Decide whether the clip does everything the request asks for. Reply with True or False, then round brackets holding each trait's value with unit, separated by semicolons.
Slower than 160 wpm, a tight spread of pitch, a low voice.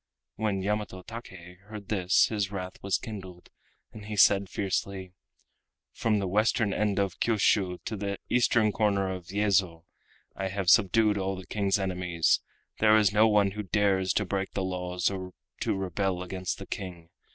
False (165 wpm; 2.2 semitones; 95 Hz)